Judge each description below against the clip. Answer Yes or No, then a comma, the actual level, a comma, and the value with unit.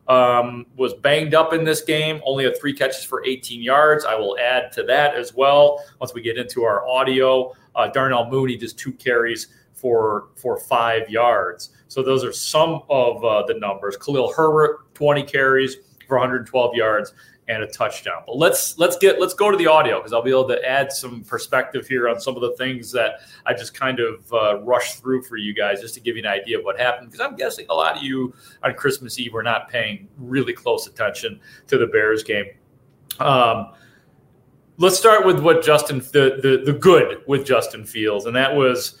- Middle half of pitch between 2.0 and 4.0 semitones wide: Yes, average, 3.6 semitones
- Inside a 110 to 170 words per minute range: No, fast, 205 wpm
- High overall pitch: No, low, 130 Hz